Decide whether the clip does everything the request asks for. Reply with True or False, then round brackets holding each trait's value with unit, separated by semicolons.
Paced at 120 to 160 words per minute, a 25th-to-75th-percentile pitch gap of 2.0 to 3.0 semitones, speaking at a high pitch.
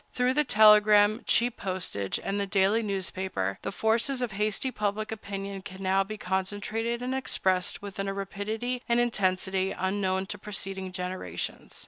True (150 wpm; 2.6 semitones; 200 Hz)